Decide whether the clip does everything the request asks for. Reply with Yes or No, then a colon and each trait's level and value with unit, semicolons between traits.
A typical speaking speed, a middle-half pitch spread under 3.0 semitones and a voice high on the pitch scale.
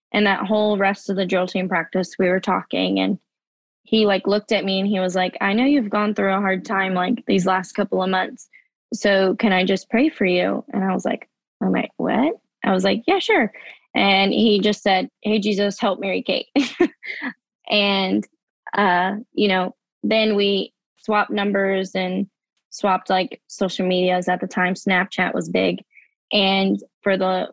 Yes: average, 190 wpm; narrow, 2.4 semitones; high, 195 Hz